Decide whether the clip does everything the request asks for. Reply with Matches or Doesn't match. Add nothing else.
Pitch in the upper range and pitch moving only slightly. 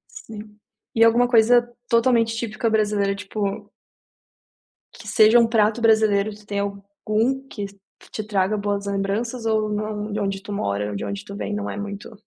Matches